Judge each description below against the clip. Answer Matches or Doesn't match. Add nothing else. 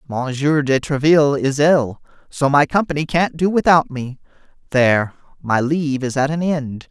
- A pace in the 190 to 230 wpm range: Doesn't match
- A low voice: Doesn't match